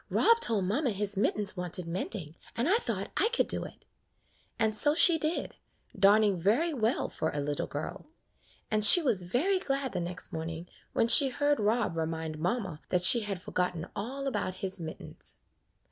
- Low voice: No, high, 205 Hz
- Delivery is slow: No, average, 185 wpm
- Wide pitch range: Yes, wide, 6.9 semitones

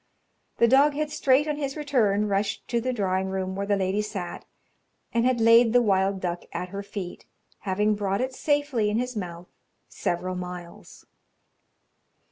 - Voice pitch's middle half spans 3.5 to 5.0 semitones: Yes, average, 4.7 semitones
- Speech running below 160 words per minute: No, average, 165 wpm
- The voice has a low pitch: No, high, 210 Hz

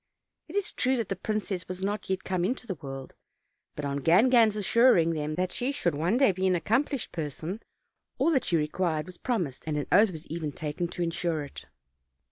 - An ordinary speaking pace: No, fast, 210 wpm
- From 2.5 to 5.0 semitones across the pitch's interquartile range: No, wide, 5.4 semitones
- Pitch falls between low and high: Yes, medium, 180 Hz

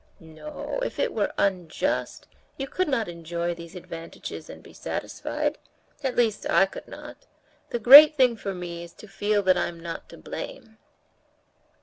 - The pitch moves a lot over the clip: Yes, wide, 6.1 semitones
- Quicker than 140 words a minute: Yes, average, 155 wpm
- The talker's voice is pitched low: No, high, 195 Hz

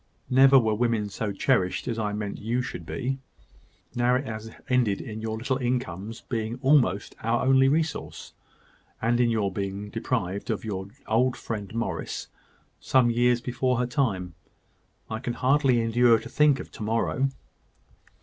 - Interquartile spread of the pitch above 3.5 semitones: No, average, 2.9 semitones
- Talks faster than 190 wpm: No, average, 165 wpm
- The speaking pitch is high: No, low, 115 Hz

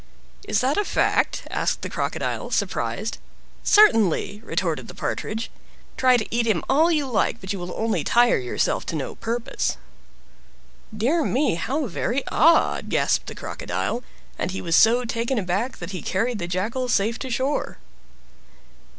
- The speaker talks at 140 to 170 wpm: Yes, average, 160 wpm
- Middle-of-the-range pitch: No, high, 230 Hz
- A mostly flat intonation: No, average, 4.8 semitones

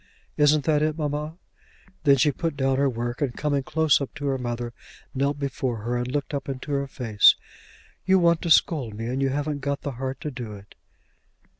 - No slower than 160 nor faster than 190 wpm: No, fast, 205 wpm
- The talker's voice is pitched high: No, medium, 140 Hz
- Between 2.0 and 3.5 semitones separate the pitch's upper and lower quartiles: Yes, average, 2.9 semitones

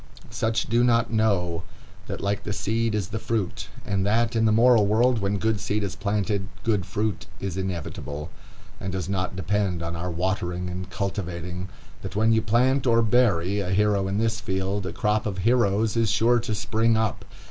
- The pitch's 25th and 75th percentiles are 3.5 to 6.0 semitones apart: No, average, 3.0 semitones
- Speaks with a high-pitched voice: No, low, 105 Hz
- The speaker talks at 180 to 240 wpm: Yes, average, 190 wpm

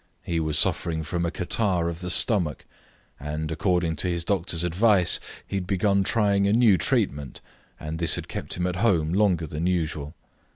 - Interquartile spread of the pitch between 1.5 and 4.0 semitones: Yes, average, 3.3 semitones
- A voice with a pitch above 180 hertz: No, very low, 85 Hz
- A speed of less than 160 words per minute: No, average, 180 wpm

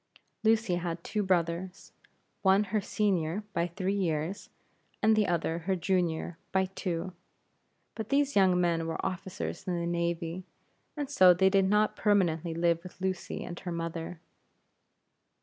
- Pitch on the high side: No, medium, 180 Hz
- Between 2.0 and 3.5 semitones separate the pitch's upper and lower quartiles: Yes, narrow, 2.6 semitones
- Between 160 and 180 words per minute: No, average, 150 wpm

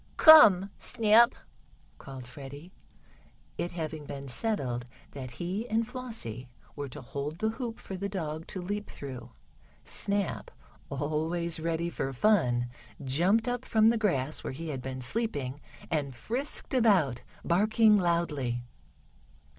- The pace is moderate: No, slow, 130 wpm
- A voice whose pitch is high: No, medium, 170 Hz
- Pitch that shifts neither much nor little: No, wide, 7.9 semitones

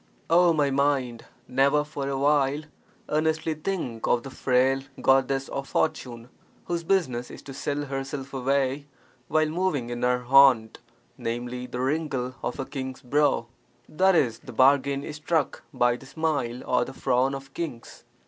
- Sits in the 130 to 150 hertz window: Yes, low, 135 Hz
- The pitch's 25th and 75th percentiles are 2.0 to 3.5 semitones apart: Yes, average, 2.9 semitones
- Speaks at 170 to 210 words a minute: No, average, 155 wpm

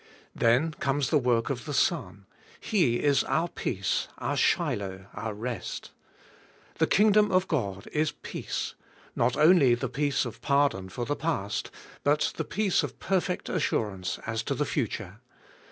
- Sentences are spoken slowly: No, average, 150 wpm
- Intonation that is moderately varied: No, wide, 6.2 semitones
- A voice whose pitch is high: No, low, 135 Hz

